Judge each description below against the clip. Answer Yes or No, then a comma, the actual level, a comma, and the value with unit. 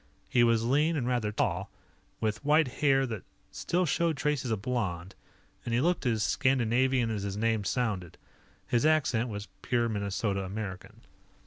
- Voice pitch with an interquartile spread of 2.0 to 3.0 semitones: No, average, 4.2 semitones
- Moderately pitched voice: No, low, 115 Hz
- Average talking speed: Yes, average, 155 wpm